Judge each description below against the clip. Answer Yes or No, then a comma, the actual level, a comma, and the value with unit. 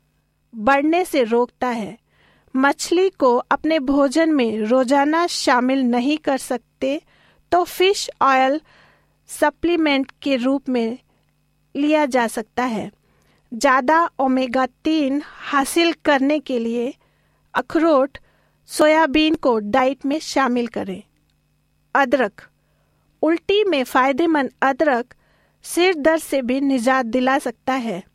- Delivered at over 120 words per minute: No, slow, 110 wpm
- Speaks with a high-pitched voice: Yes, very high, 275 Hz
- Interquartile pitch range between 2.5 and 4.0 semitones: Yes, average, 3.7 semitones